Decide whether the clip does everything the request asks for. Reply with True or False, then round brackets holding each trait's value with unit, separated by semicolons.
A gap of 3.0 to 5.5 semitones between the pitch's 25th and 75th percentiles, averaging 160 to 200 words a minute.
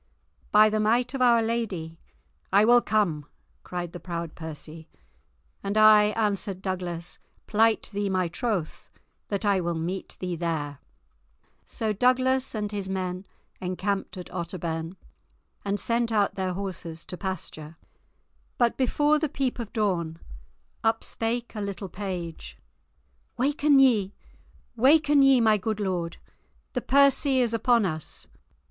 False (4.8 semitones; 135 wpm)